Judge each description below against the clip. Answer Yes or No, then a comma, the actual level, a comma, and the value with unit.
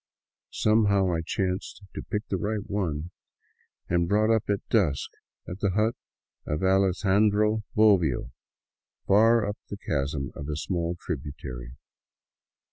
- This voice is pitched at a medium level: No, very low, 95 Hz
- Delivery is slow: Yes, slow, 130 wpm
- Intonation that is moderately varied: Yes, average, 4.8 semitones